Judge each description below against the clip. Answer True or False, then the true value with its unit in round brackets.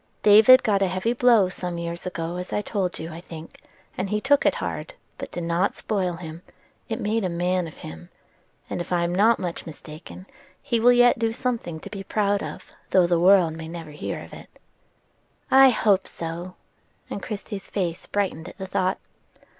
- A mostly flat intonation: False (3.8 semitones)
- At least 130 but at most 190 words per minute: False (200 wpm)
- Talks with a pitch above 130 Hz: True (185 Hz)